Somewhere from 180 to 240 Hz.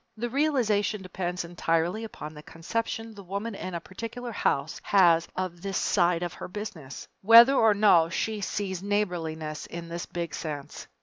Yes: medium, 185 Hz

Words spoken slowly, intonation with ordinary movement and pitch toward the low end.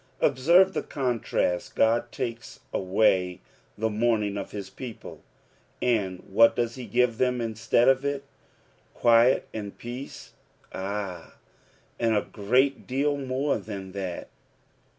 Yes: slow, 130 wpm; average, 4.1 semitones; low, 115 Hz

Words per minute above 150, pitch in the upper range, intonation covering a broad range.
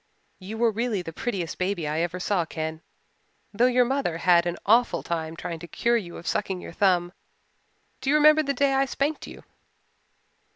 Yes: average, 190 wpm; high, 195 Hz; wide, 6.2 semitones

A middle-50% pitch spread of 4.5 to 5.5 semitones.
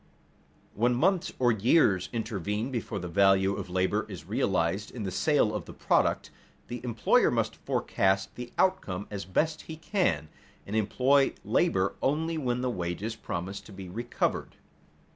Yes: average, 4.8 semitones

